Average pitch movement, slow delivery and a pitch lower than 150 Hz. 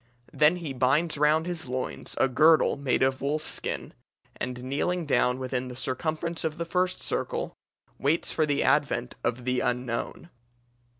No: average, 3.9 semitones; average, 160 wpm; medium, 140 Hz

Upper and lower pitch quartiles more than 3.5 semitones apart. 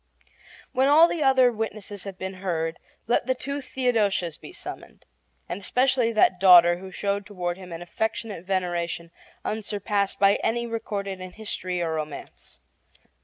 Yes: average, 4.2 semitones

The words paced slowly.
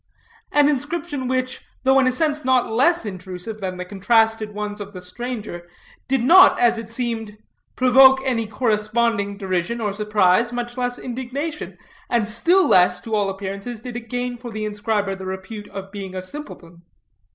No: average, 170 wpm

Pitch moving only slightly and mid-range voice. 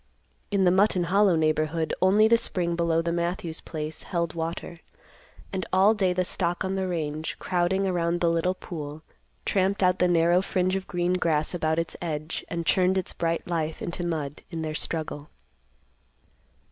Yes: narrow, 2.3 semitones; medium, 170 Hz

